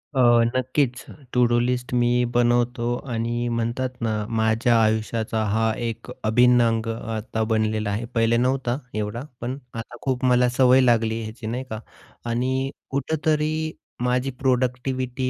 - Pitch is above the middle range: No, low, 120 Hz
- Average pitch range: No, narrow, 2.1 semitones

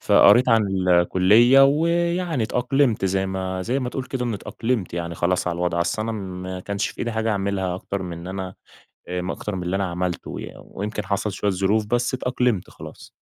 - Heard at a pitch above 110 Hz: No, low, 100 Hz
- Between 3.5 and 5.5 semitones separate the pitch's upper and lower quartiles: Yes, average, 4.7 semitones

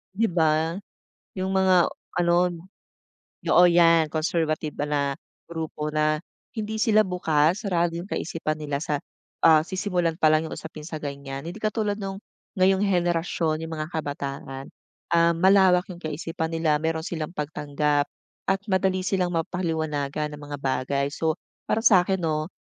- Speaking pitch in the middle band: Yes, medium, 165 Hz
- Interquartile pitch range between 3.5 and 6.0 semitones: No, average, 3.0 semitones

